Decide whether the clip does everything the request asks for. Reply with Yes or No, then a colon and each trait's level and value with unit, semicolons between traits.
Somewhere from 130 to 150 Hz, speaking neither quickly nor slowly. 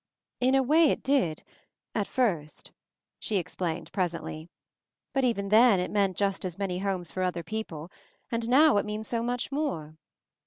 No: high, 200 Hz; average, 170 wpm